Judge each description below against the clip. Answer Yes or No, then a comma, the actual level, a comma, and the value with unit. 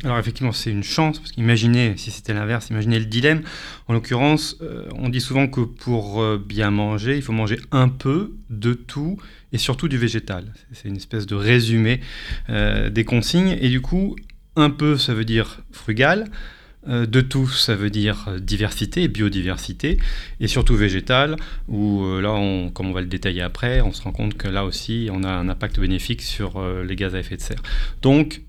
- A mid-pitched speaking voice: No, low, 115 Hz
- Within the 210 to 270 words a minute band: No, average, 200 wpm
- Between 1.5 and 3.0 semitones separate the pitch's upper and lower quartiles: No, average, 3.9 semitones